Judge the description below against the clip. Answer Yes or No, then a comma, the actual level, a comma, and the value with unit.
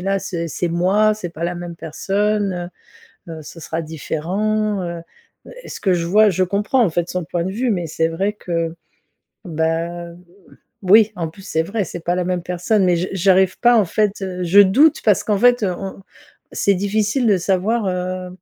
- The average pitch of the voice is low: No, medium, 185 Hz